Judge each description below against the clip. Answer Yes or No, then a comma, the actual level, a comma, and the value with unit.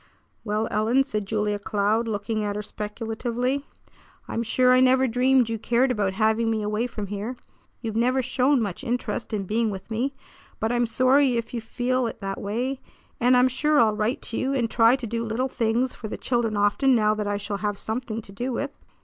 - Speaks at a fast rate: Yes, fast, 210 wpm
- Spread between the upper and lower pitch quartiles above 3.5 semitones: No, average, 3.1 semitones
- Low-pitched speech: No, high, 230 Hz